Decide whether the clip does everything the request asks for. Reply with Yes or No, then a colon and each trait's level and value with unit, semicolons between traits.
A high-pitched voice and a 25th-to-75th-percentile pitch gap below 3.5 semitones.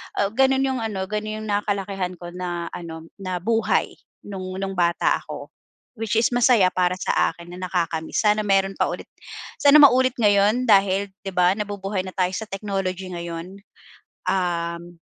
Yes: high, 195 Hz; average, 2.8 semitones